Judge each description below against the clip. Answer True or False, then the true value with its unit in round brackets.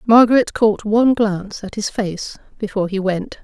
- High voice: True (210 Hz)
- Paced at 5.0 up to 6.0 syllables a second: True (5.2 syllables/s)